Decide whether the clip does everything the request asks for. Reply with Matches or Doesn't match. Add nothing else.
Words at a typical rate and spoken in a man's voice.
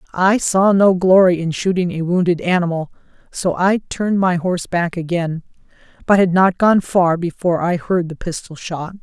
Doesn't match